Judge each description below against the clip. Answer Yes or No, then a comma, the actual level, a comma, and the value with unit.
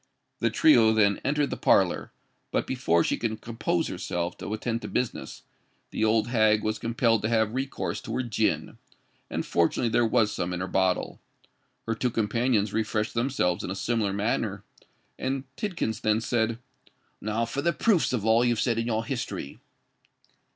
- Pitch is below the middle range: Yes, low, 110 Hz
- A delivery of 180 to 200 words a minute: No, average, 170 wpm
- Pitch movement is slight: Yes, narrow, 2.2 semitones